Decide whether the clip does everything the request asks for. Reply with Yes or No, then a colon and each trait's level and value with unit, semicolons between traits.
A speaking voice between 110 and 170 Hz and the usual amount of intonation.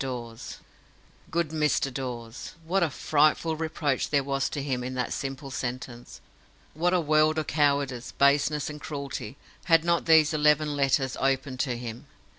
Yes: medium, 140 Hz; average, 3.0 semitones